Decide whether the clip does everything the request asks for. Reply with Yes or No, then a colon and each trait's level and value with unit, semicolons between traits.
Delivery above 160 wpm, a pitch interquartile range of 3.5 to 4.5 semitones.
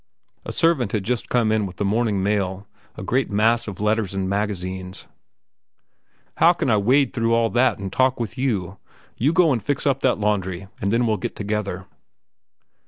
Yes: average, 180 wpm; average, 3.8 semitones